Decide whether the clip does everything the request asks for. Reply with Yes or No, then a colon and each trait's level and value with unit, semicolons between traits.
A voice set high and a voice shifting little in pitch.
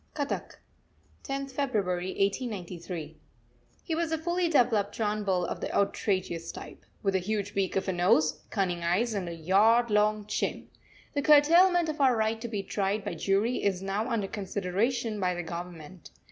No: high, 205 Hz; average, 4.7 semitones